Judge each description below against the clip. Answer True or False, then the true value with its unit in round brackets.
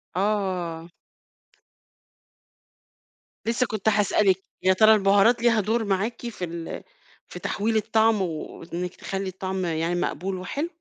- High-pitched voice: True (195 Hz)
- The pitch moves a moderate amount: True (3.3 semitones)